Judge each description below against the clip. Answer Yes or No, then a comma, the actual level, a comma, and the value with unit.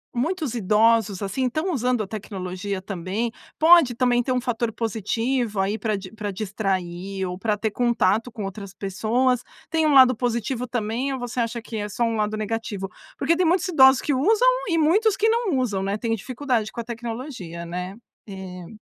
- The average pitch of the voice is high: Yes, high, 225 Hz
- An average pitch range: Yes, average, 4.3 semitones